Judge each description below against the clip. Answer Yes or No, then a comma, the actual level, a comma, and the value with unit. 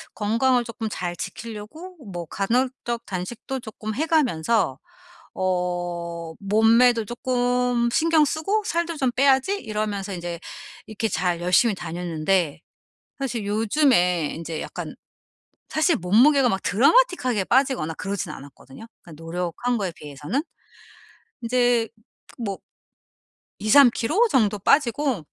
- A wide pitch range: Yes, wide, 6.2 semitones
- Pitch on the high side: Yes, high, 220 Hz